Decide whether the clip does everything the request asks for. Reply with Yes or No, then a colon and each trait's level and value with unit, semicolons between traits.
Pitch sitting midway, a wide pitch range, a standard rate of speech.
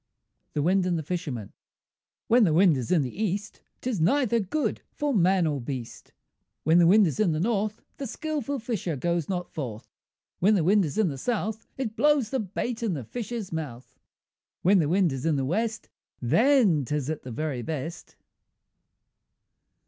Yes: medium, 180 Hz; wide, 6.4 semitones; average, 180 wpm